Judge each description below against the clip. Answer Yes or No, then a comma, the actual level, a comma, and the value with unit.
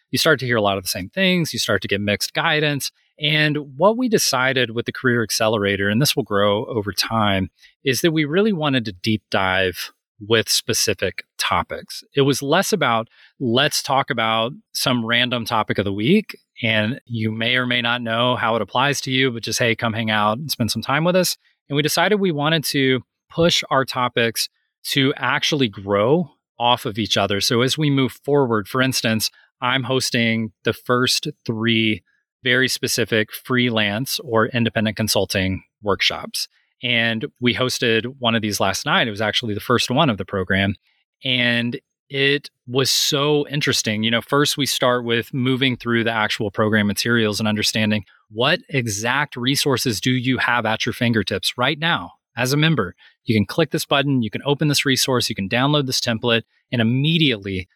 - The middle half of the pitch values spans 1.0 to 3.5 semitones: No, average, 4.0 semitones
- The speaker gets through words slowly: No, average, 185 wpm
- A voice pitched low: Yes, low, 120 Hz